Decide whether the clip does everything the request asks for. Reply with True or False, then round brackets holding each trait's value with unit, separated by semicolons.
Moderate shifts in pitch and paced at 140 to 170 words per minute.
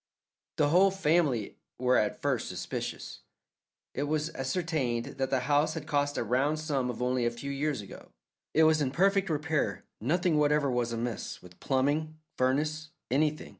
True (3.6 semitones; 160 wpm)